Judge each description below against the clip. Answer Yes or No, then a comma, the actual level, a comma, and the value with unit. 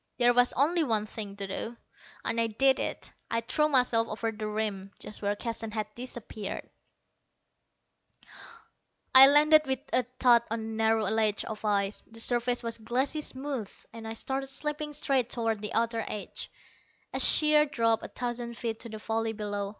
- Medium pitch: No, high, 230 Hz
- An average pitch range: Yes, average, 3.1 semitones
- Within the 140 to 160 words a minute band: No, average, 175 wpm